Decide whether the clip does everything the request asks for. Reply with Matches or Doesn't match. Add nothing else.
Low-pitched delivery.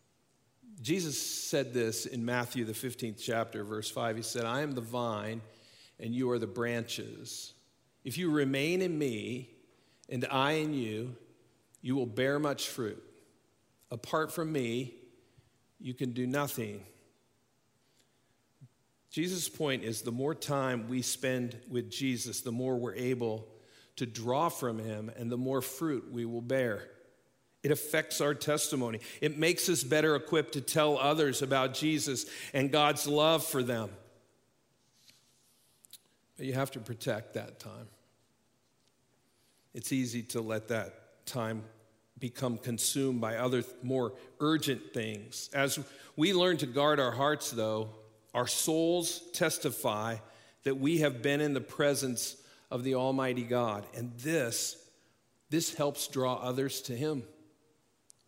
Matches